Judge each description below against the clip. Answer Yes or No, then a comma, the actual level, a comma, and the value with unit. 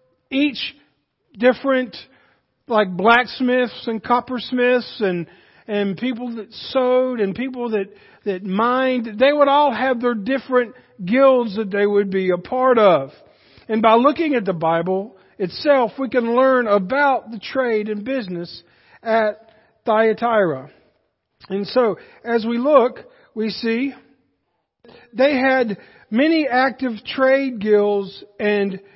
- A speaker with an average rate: No, slow, 125 wpm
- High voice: Yes, high, 235 Hz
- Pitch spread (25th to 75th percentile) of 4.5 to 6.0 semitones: No, average, 3.8 semitones